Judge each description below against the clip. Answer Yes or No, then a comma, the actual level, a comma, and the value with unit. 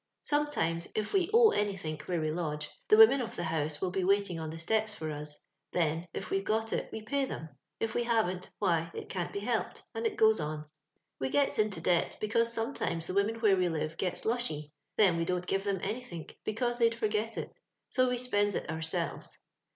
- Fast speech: Yes, fast, 210 wpm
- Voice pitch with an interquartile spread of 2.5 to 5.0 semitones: No, wide, 5.4 semitones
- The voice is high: Yes, high, 195 Hz